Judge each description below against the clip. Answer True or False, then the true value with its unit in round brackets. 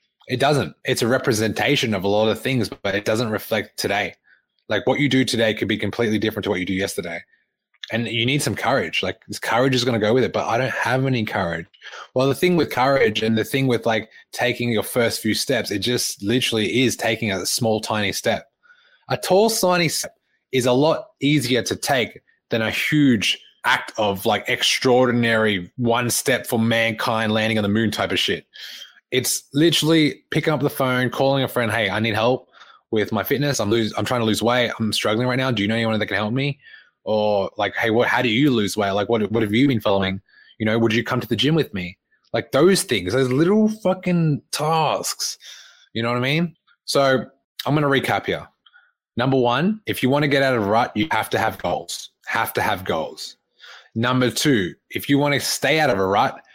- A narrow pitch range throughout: False (4.2 semitones)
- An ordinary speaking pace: False (225 wpm)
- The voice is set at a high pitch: False (120 Hz)